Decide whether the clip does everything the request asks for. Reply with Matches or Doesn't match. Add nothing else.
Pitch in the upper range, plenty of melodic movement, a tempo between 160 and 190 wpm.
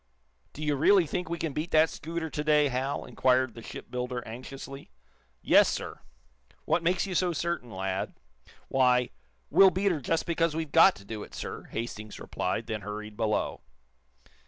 Doesn't match